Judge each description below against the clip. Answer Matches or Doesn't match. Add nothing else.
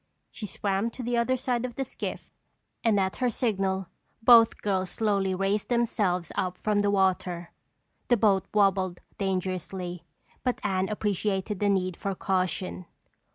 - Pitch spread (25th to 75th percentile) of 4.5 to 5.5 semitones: Doesn't match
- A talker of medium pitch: Doesn't match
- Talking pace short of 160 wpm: Matches